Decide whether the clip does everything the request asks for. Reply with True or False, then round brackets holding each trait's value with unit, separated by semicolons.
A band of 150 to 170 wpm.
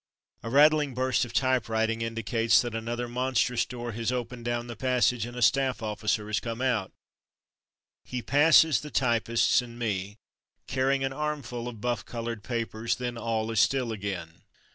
True (165 wpm)